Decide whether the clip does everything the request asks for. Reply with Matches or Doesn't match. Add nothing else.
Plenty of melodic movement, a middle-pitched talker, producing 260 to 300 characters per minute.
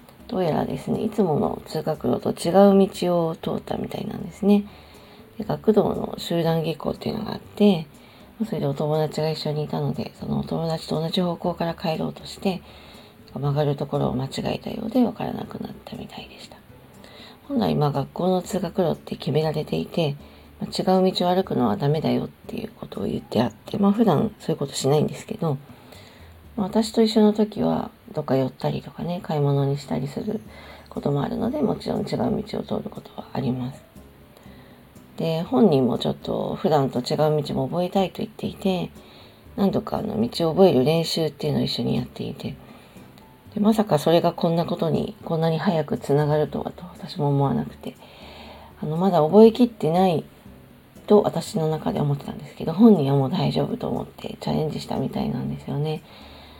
Doesn't match